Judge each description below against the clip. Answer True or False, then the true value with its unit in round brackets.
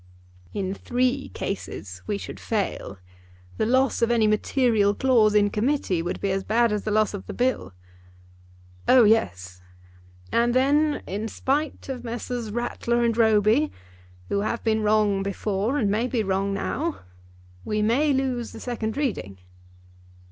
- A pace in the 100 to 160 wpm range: True (150 wpm)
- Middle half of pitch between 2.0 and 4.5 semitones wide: True (3.6 semitones)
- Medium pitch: False (220 Hz)